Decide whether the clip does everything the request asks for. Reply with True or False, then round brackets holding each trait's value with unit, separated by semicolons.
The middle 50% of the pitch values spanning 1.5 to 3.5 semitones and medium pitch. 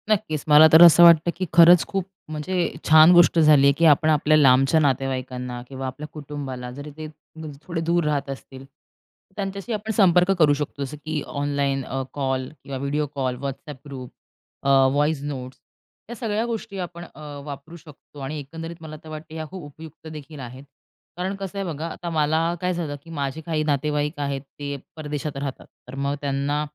True (3.1 semitones; 150 Hz)